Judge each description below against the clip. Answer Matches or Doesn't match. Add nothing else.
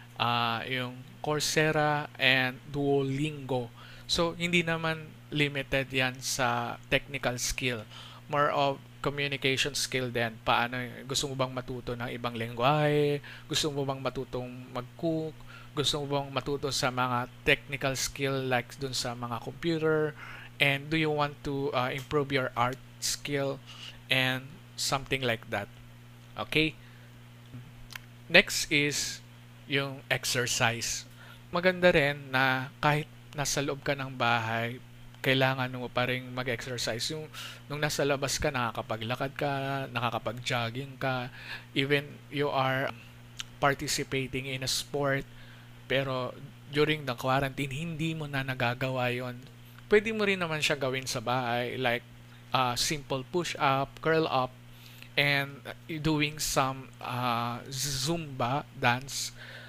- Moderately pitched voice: Doesn't match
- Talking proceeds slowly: Doesn't match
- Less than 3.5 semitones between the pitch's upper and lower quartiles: Matches